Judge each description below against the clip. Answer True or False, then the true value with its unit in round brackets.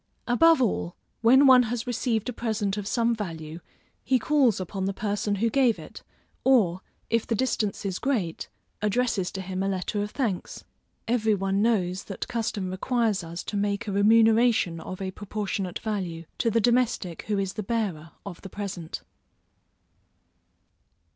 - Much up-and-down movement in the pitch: False (3.5 semitones)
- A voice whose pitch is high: True (210 Hz)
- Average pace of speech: True (160 wpm)